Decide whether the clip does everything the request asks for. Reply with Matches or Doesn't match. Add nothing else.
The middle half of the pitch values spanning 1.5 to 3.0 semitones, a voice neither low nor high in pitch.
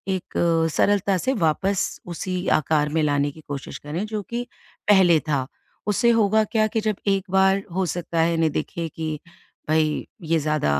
Doesn't match